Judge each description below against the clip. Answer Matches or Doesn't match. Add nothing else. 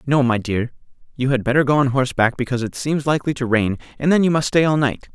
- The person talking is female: Doesn't match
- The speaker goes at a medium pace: Doesn't match